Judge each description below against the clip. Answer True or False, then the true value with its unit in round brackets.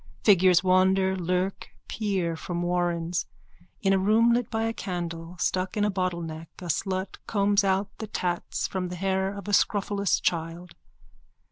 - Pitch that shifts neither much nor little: False (2.3 semitones)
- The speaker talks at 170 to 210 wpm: False (155 wpm)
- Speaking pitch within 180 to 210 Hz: True (185 Hz)